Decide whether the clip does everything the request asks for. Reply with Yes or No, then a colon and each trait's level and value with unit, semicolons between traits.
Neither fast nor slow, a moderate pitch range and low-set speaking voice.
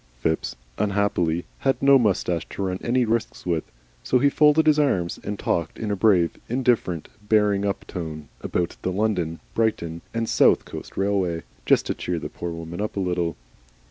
Yes: average, 175 wpm; average, 4.6 semitones; low, 100 Hz